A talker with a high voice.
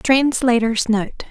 Yes: high, 240 Hz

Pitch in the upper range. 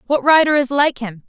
Yes: very high, 265 Hz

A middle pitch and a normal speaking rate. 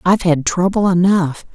Yes: medium, 180 Hz; average, 155 wpm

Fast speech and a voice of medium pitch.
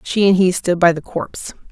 Yes: fast, 245 wpm; medium, 180 Hz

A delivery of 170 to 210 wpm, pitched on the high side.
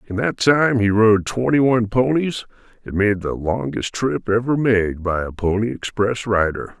No: average, 175 wpm; low, 110 Hz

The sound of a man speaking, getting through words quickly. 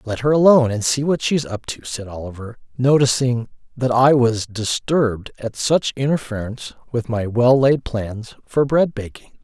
No: male; average, 170 wpm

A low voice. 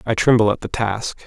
Yes: low, 110 Hz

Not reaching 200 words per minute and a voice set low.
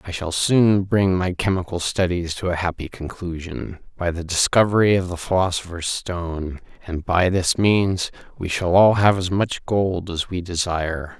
Yes: average, 170 wpm; very low, 90 Hz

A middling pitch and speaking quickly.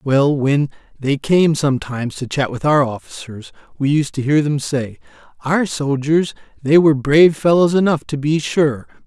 No: medium, 145 Hz; average, 170 wpm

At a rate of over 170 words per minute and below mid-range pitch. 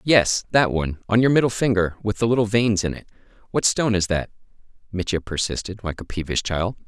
Yes: average, 200 wpm; low, 100 Hz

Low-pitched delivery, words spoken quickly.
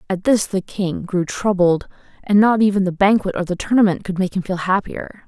No: high, 190 Hz; fast, 215 wpm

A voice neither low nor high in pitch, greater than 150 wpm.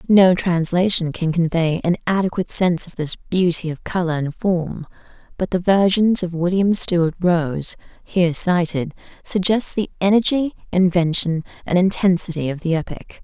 No: medium, 175 Hz; average, 145 wpm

